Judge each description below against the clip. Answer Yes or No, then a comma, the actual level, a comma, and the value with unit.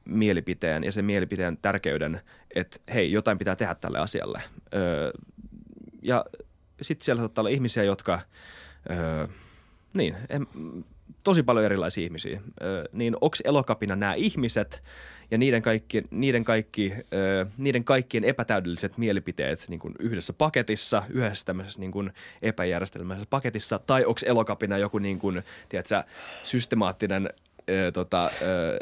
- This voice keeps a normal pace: Yes, average, 130 wpm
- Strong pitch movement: No, average, 3.7 semitones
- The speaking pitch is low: Yes, low, 105 Hz